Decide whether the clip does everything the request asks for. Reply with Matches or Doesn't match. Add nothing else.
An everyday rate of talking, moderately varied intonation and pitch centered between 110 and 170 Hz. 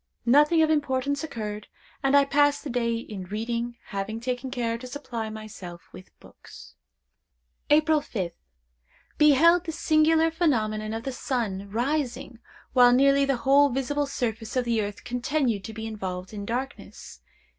Doesn't match